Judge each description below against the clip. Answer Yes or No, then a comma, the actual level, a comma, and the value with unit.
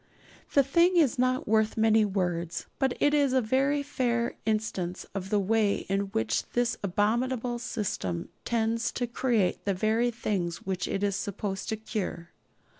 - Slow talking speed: No, average, 160 wpm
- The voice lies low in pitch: No, high, 220 Hz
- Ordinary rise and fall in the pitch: Yes, average, 3.9 semitones